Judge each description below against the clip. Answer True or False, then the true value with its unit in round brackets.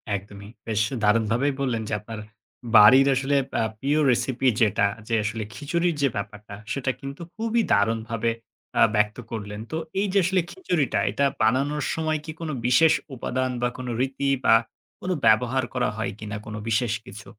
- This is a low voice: True (125 Hz)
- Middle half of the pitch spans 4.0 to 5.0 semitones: True (4.6 semitones)